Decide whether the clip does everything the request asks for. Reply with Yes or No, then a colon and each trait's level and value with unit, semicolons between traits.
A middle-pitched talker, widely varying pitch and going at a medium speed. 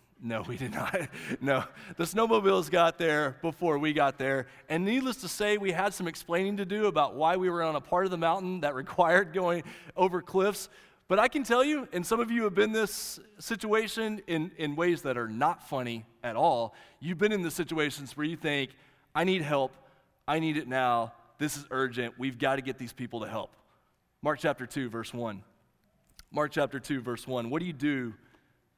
No: medium, 155 Hz; wide, 5.7 semitones; fast, 210 wpm